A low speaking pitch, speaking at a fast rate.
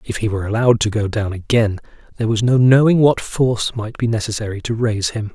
Yes: low, 110 Hz; fast, 225 wpm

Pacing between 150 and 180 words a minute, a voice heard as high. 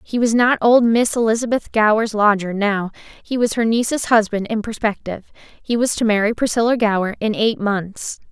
Yes: average, 175 wpm; high, 220 Hz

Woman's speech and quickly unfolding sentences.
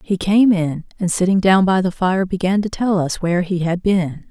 Yes: female; fast, 235 wpm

